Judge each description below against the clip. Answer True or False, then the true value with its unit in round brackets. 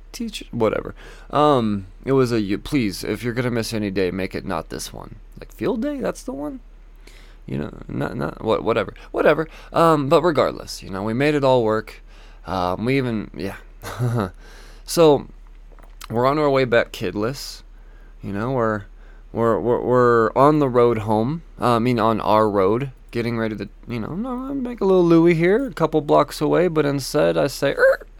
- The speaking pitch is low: True (125 Hz)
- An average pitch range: False (6.0 semitones)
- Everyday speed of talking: True (185 wpm)